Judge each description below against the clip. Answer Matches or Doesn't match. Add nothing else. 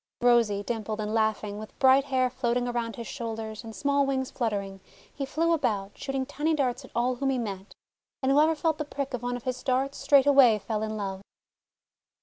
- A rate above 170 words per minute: Matches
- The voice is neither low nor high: Doesn't match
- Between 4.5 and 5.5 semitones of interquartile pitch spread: Doesn't match